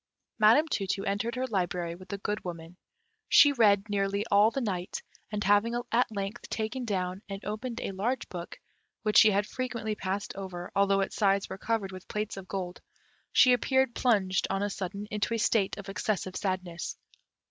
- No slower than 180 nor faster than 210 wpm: Yes, average, 185 wpm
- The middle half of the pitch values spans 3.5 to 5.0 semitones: No, average, 2.7 semitones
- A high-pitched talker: Yes, high, 200 Hz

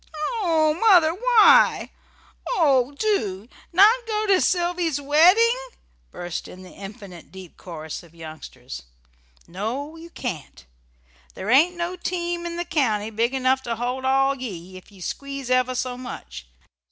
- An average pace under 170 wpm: Yes, average, 140 wpm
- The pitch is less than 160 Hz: No, very high, 270 Hz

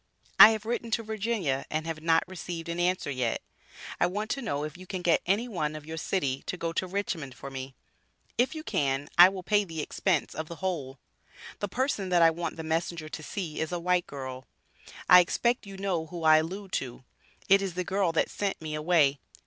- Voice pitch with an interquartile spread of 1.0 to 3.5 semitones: No, average, 4.1 semitones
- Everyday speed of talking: No, fast, 220 wpm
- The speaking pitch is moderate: Yes, medium, 170 Hz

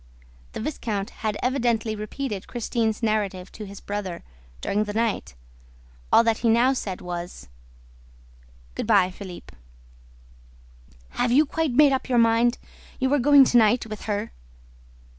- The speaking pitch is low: No, high, 225 Hz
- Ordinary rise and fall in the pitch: Yes, average, 3.2 semitones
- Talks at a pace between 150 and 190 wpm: No, average, 140 wpm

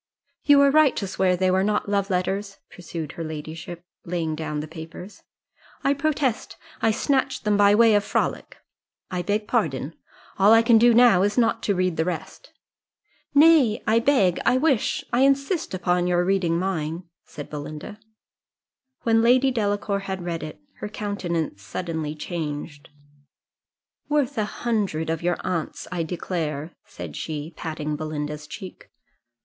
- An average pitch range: No, wide, 5.7 semitones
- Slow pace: No, average, 155 wpm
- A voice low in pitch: No, medium, 185 Hz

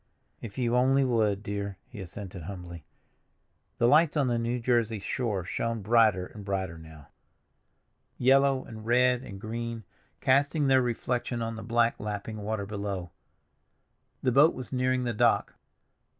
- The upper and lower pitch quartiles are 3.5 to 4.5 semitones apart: Yes, average, 3.8 semitones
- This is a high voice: No, low, 115 Hz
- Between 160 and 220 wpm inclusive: No, average, 150 wpm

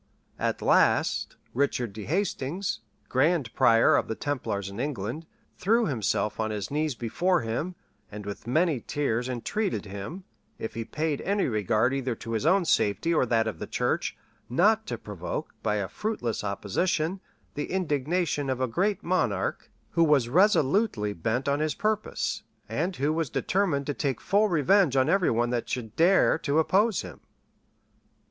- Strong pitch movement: Yes, wide, 7.6 semitones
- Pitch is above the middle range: No, medium, 140 Hz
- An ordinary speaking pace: Yes, average, 165 wpm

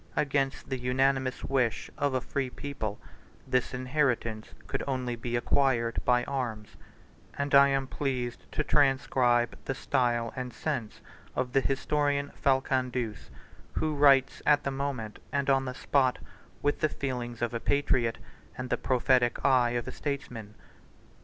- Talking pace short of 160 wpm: Yes, average, 145 wpm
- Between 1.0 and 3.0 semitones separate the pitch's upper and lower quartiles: Yes, narrow, 2.4 semitones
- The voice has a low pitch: Yes, low, 130 Hz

